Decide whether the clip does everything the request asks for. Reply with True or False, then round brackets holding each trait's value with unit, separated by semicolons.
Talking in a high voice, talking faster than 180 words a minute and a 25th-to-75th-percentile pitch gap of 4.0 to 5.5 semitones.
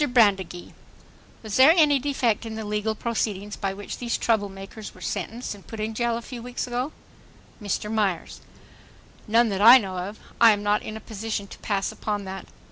False (215 Hz; 195 wpm; 2.7 semitones)